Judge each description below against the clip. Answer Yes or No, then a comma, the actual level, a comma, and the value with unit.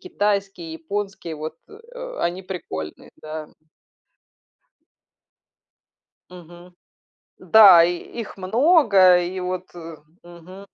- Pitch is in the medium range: Yes, medium, 180 Hz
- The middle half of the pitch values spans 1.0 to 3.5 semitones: Yes, average, 2.8 semitones